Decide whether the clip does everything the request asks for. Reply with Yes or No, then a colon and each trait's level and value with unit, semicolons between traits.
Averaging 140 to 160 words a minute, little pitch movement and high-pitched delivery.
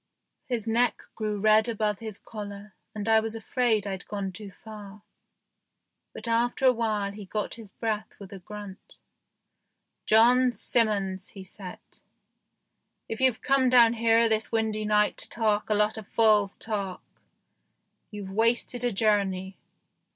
Yes: average, 150 wpm; narrow, 2.1 semitones; high, 215 Hz